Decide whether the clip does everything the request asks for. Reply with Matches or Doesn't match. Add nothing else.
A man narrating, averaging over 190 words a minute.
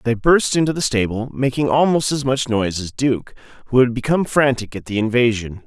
Matches